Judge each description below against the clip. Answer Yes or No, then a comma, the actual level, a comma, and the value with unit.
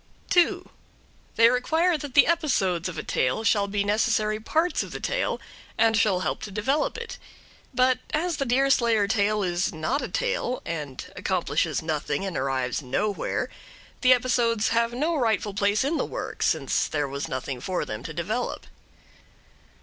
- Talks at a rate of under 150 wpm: No, average, 165 wpm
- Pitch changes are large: Yes, wide, 6.4 semitones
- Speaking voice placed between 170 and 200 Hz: No, high, 220 Hz